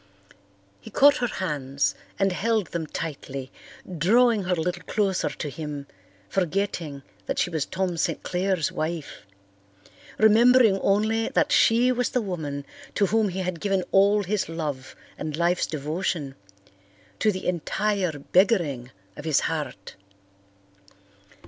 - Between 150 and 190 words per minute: No, slow, 135 wpm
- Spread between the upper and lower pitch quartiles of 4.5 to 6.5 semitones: Yes, average, 5.1 semitones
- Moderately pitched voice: Yes, medium, 180 Hz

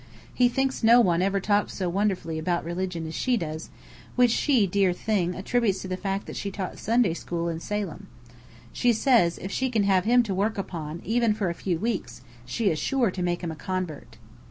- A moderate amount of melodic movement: Yes, average, 4.4 semitones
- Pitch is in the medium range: No, high, 195 Hz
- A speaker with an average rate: No, fast, 210 wpm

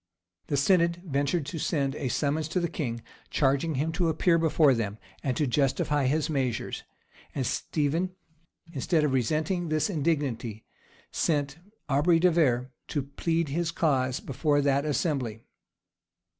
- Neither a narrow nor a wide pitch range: Yes, average, 3.4 semitones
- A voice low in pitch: No, medium, 145 Hz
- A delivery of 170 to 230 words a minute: No, average, 145 wpm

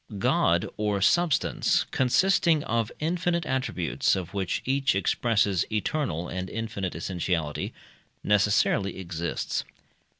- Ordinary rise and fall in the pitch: No, wide, 6.4 semitones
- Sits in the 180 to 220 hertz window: No, low, 105 Hz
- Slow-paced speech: Yes, slow, 100 wpm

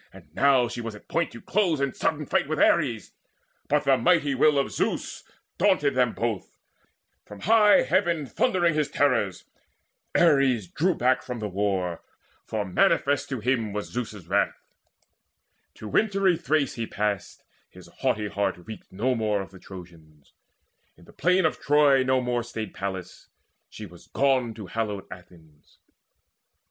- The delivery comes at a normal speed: Yes, average, 155 wpm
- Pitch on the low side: Yes, low, 120 Hz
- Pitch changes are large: Yes, wide, 6.0 semitones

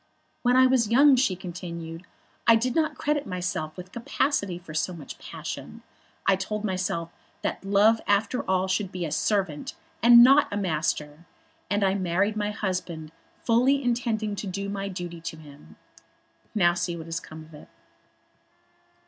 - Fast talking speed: No, average, 165 wpm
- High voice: Yes, high, 195 Hz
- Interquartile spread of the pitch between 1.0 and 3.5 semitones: No, average, 4.7 semitones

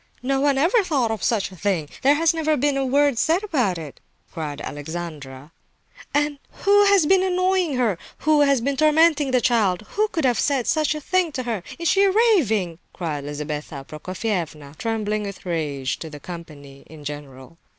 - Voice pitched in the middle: No, high, 235 Hz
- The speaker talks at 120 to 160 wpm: No, average, 180 wpm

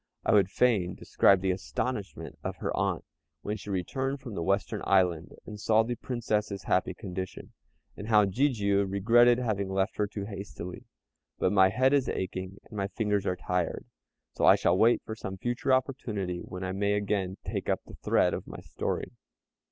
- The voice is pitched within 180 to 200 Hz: No, low, 100 Hz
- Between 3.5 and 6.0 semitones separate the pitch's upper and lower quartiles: No, average, 3.0 semitones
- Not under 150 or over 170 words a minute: No, average, 185 wpm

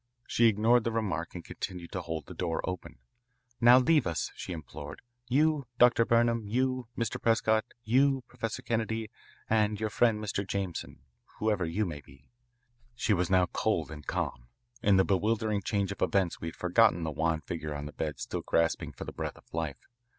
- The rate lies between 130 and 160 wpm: No, average, 185 wpm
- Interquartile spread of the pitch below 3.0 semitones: No, wide, 5.5 semitones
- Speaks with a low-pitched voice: Yes, low, 100 Hz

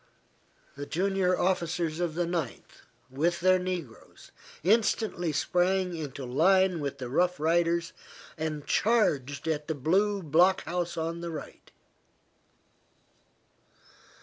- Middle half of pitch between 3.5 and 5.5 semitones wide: No, average, 2.9 semitones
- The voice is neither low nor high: Yes, medium, 170 Hz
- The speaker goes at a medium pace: No, slow, 115 wpm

